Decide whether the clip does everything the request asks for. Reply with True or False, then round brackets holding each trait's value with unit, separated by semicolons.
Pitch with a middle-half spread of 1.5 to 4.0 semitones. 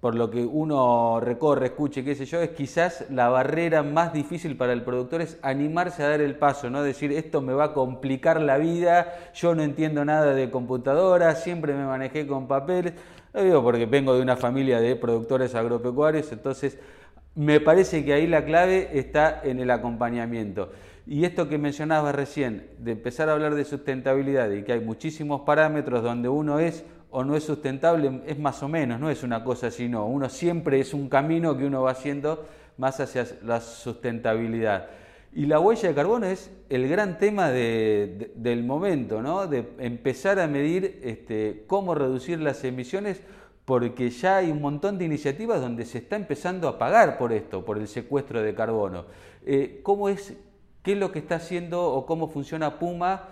False (4.5 semitones)